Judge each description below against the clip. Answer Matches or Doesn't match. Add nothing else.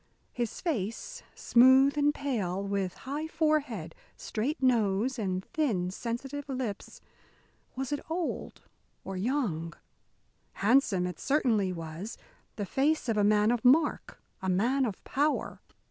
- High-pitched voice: Matches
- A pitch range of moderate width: Doesn't match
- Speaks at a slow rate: Matches